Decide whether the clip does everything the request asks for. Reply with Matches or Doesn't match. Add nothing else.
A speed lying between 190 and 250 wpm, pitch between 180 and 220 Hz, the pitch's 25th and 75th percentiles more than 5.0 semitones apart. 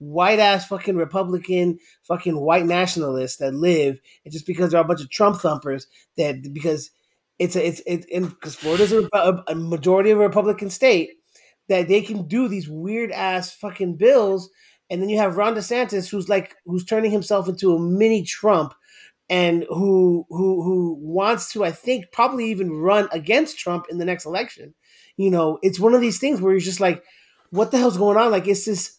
Doesn't match